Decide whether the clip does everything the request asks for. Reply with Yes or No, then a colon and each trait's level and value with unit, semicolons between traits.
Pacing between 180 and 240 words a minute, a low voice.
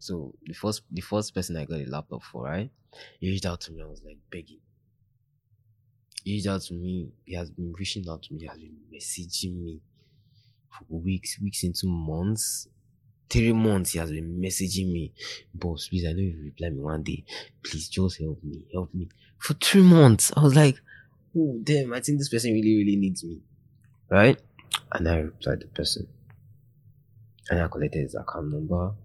Yes: average, 195 wpm; very low, 95 Hz